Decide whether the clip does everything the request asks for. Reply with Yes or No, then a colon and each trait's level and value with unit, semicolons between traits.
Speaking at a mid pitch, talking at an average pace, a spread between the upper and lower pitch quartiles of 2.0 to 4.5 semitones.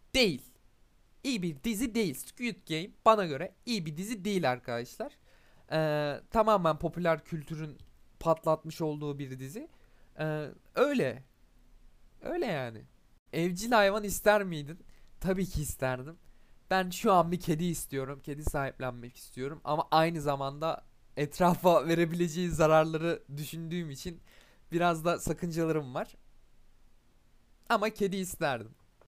Yes: medium, 165 Hz; average, 120 wpm; average, 3.9 semitones